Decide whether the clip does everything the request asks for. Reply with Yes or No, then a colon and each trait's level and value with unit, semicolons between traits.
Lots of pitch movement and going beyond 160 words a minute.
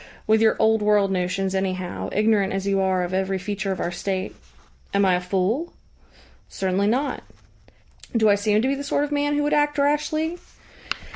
Yes: wide, 6.3 semitones; average, 190 wpm